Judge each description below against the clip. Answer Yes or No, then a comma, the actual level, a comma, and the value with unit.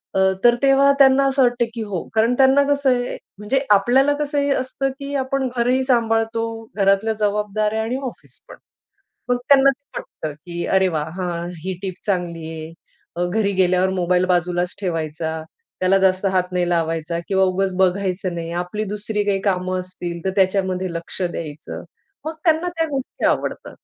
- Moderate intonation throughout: No, wide, 5.7 semitones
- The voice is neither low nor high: No, high, 195 Hz